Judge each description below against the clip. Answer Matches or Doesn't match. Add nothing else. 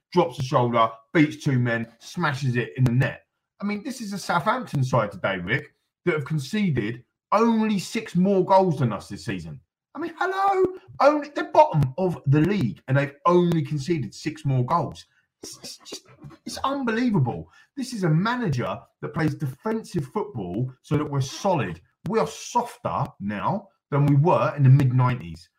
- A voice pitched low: Doesn't match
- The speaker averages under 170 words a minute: Doesn't match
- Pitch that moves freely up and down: Matches